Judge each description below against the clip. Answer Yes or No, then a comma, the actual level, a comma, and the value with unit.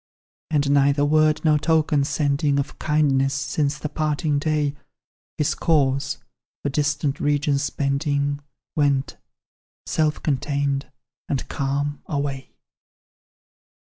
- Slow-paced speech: Yes, slow, 105 wpm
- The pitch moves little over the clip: Yes, narrow, 1.2 semitones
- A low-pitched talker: No, medium, 145 Hz